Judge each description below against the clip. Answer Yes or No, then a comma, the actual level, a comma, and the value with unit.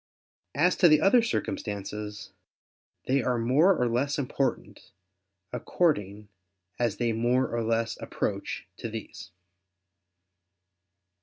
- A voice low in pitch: Yes, low, 120 Hz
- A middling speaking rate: No, slow, 105 wpm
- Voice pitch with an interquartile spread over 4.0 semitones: Yes, average, 4.5 semitones